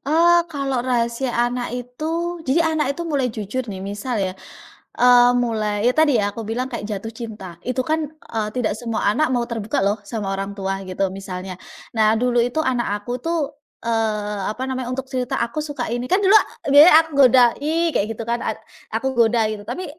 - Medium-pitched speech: No, high, 240 Hz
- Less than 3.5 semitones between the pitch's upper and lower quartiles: No, average, 3.8 semitones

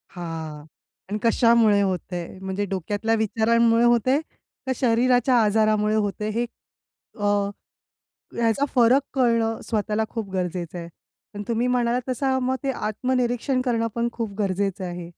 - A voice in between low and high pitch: No, high, 225 Hz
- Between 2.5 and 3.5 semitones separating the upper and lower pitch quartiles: Yes, average, 3.0 semitones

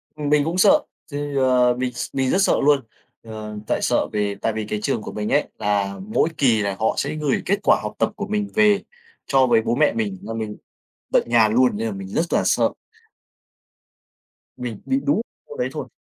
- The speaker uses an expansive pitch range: Yes, wide, 5.8 semitones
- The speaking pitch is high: No, low, 125 Hz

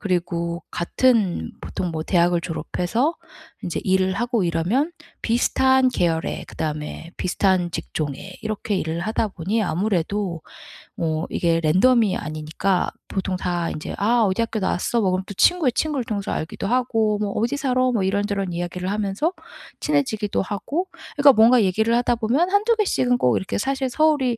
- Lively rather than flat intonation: Yes, wide, 5.7 semitones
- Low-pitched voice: No, high, 200 Hz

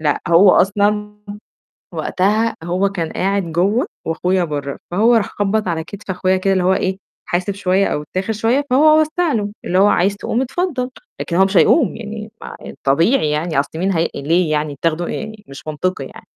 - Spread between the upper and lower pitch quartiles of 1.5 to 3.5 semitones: No, average, 4.1 semitones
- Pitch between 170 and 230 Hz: Yes, high, 190 Hz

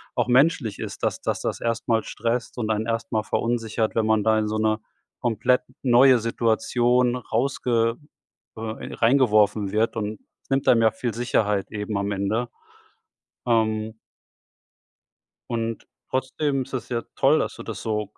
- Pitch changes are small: Yes, narrow, 2.0 semitones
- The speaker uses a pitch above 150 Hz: No, low, 115 Hz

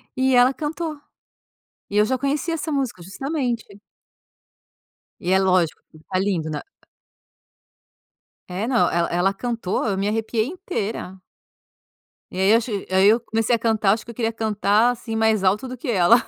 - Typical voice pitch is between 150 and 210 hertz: No, high, 220 Hz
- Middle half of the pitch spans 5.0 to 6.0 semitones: No, average, 4.5 semitones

